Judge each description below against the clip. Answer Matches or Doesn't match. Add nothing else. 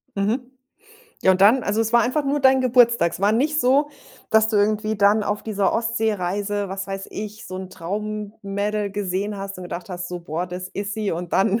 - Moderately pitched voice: Doesn't match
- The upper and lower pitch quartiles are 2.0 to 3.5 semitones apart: Matches